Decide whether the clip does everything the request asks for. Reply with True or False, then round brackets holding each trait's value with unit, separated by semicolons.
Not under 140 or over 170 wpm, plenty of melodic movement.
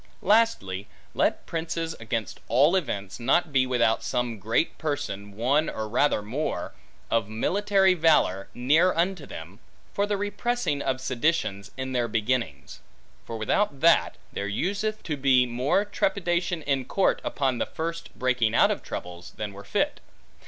True (150 wpm; 7.2 semitones)